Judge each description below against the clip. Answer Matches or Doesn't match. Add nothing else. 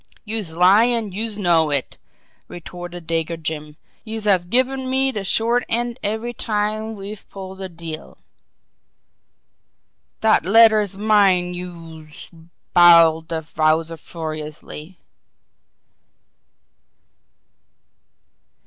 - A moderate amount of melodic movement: Matches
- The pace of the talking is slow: Matches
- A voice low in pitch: Doesn't match